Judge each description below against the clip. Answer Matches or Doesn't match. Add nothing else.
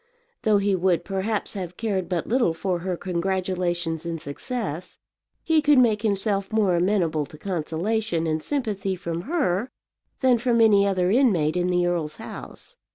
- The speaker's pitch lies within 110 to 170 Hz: Doesn't match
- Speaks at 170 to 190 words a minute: Doesn't match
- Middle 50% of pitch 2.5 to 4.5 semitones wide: Matches